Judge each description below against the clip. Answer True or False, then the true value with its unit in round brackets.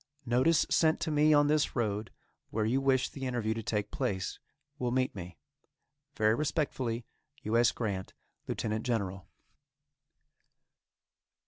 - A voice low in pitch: True (120 Hz)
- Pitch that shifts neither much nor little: True (4.0 semitones)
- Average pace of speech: False (130 wpm)